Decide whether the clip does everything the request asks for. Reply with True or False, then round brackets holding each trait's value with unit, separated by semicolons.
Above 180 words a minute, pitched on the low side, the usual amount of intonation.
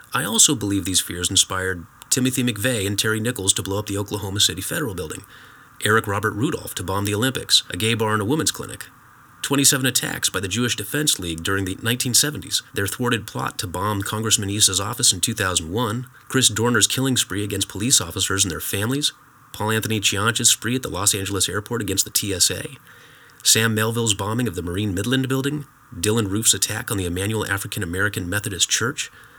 True (190 wpm; 110 Hz; 3.8 semitones)